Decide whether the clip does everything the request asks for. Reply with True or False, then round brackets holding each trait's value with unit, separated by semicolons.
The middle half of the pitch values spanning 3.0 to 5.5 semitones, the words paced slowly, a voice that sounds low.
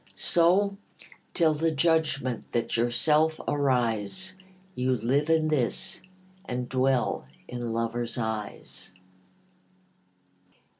True (5.1 semitones; 90 wpm; 130 Hz)